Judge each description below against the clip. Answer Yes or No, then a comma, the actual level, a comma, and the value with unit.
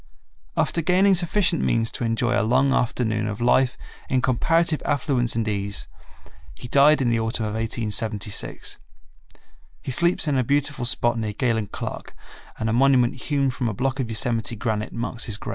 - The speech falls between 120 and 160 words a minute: No, average, 175 wpm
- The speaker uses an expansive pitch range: No, average, 3.5 semitones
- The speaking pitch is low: Yes, low, 120 Hz